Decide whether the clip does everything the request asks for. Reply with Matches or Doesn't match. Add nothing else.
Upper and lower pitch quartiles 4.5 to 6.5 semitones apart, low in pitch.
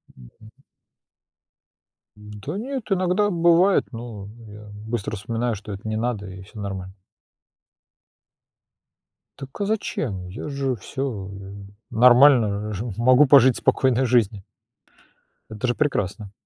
Matches